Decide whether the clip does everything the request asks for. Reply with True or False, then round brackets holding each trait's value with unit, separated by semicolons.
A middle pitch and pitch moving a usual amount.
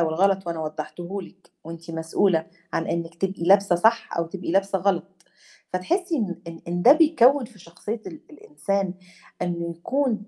True (180 Hz; 3.2 semitones)